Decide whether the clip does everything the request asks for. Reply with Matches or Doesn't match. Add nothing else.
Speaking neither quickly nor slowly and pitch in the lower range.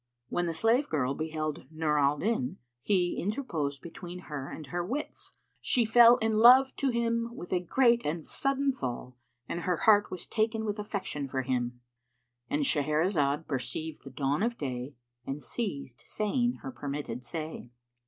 Doesn't match